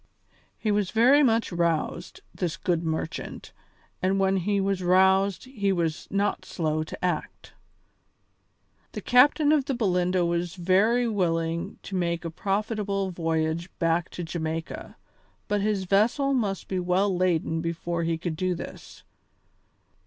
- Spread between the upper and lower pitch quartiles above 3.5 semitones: No, average, 3.2 semitones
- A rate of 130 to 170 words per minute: Yes, average, 140 wpm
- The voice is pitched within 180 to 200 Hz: Yes, medium, 185 Hz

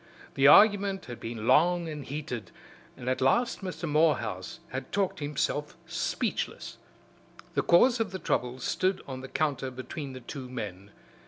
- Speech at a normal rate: Yes, average, 155 wpm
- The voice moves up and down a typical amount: No, wide, 5.8 semitones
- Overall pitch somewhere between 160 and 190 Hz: No, medium, 145 Hz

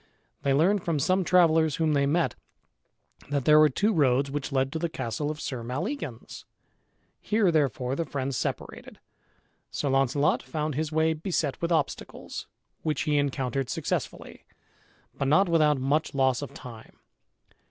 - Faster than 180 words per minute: No, average, 155 wpm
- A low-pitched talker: No, medium, 150 Hz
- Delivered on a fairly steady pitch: No, average, 3.0 semitones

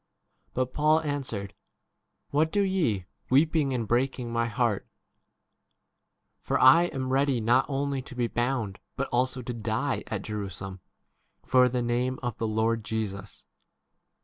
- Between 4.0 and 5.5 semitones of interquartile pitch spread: No, average, 3.5 semitones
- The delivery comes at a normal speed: Yes, average, 145 wpm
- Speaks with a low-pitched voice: Yes, low, 125 Hz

